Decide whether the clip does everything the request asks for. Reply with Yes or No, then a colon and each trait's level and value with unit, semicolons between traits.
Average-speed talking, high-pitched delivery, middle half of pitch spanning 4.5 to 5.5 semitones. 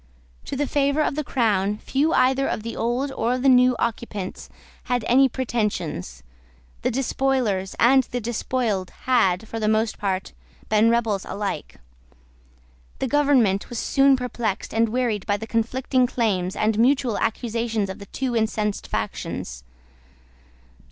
No: average, 145 wpm; high, 230 Hz; average, 3.7 semitones